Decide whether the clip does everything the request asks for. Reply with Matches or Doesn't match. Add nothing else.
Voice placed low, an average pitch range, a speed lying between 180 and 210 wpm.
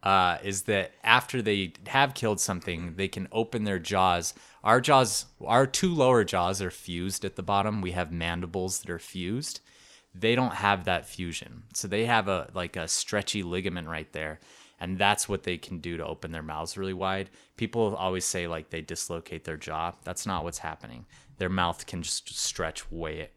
Matches